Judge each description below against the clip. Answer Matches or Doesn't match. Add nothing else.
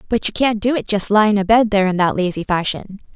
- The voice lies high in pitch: Matches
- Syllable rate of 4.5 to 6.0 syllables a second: Matches